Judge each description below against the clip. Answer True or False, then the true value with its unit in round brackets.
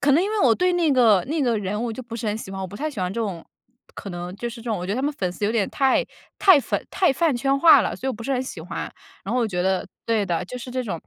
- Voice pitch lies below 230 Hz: False (235 Hz)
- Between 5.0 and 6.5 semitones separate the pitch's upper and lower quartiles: True (5.6 semitones)